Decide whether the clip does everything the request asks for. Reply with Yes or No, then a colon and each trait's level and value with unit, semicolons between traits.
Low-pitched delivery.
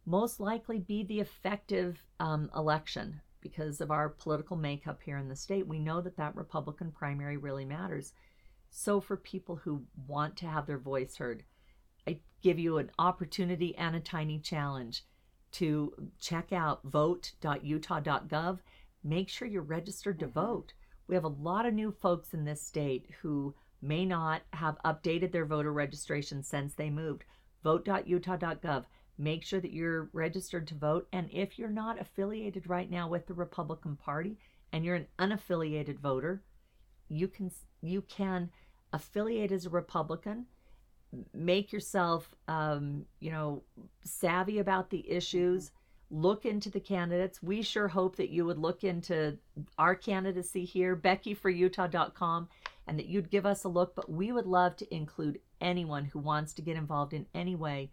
No: medium, 170 Hz